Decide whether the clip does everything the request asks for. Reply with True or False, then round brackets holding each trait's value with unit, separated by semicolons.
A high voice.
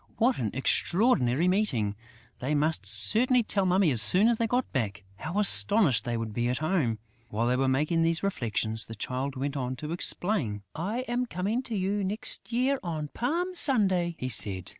False (165 Hz)